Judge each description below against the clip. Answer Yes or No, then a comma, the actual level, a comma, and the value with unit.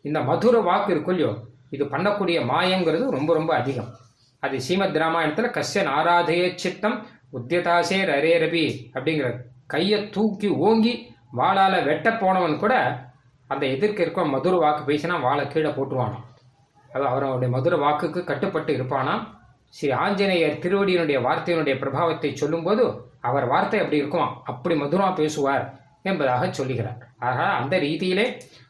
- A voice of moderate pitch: Yes, medium, 150 Hz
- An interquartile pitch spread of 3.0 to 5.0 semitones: No, wide, 5.4 semitones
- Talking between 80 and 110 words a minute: No, average, 125 wpm